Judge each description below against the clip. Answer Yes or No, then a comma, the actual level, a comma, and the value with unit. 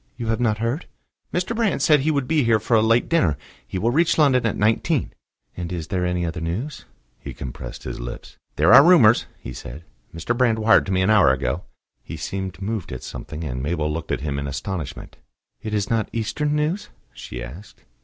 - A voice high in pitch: No, low, 105 Hz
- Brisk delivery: Yes, fast, 210 wpm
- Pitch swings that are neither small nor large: No, wide, 7.0 semitones